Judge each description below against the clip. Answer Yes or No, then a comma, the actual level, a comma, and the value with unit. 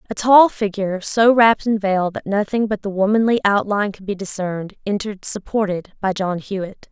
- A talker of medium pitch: No, high, 200 Hz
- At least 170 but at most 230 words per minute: Yes, average, 180 wpm